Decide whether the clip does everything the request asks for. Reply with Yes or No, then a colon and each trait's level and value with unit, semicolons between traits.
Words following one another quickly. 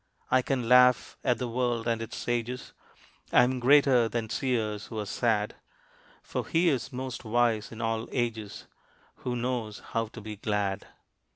No: average, 165 wpm